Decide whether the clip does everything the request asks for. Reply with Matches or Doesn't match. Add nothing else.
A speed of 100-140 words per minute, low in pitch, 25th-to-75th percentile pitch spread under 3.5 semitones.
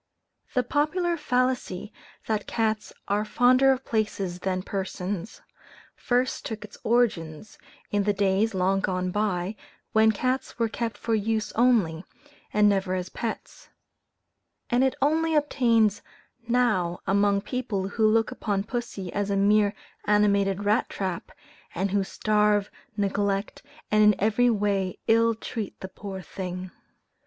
Doesn't match